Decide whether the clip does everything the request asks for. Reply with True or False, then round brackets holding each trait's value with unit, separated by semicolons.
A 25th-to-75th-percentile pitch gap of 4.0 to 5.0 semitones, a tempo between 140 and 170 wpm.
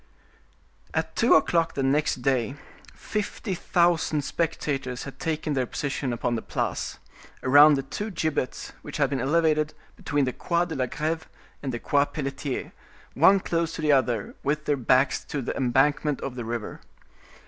False (3.3 semitones; 165 wpm)